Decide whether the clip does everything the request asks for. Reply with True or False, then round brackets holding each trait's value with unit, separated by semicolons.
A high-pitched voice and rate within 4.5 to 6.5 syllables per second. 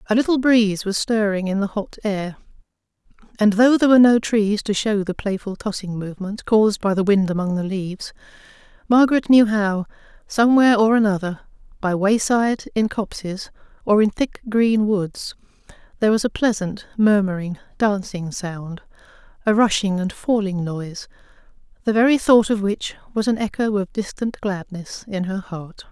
True (205 Hz; 5.1 syllables/s)